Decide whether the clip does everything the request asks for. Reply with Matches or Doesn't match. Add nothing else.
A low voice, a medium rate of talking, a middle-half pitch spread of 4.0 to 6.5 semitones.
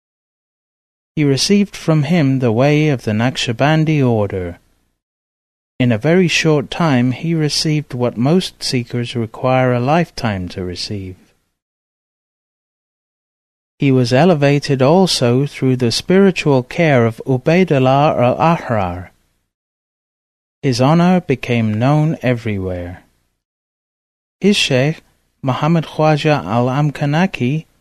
Doesn't match